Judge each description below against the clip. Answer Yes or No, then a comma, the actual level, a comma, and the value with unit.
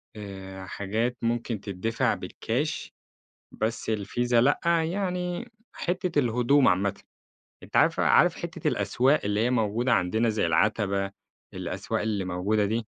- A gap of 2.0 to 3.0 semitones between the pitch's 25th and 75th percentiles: No, average, 3.8 semitones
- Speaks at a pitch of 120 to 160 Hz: No, low, 110 Hz